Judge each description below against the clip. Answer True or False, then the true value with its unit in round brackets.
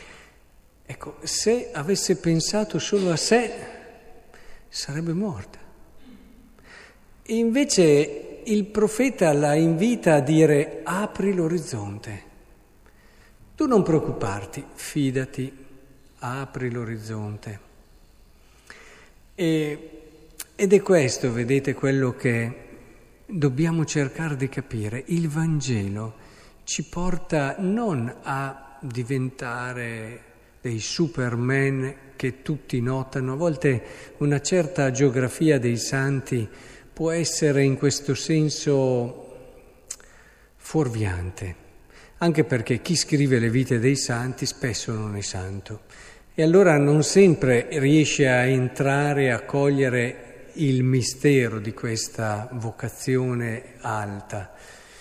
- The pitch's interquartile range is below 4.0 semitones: False (4.8 semitones)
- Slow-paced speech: True (95 wpm)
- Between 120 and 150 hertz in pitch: True (135 Hz)